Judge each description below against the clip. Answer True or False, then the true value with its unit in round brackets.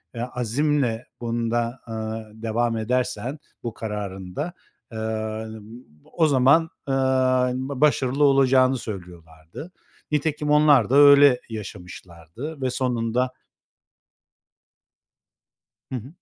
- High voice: False (120 Hz)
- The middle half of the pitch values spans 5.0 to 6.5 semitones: False (4.0 semitones)